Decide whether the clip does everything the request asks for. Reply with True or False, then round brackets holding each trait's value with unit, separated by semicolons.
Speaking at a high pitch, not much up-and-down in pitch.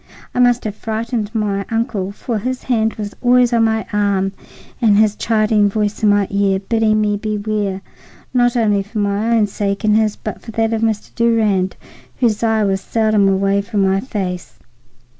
True (215 Hz; 2.0 semitones)